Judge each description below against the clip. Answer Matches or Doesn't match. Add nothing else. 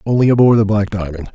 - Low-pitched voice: Matches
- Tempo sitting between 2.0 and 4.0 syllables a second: Doesn't match